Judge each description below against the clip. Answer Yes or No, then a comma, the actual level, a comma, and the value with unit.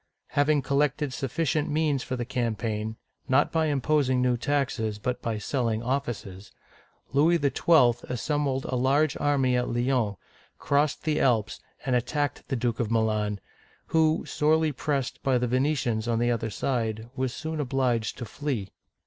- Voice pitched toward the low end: Yes, low, 130 Hz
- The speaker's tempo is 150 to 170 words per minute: Yes, average, 155 wpm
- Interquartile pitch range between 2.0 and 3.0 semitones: No, average, 3.7 semitones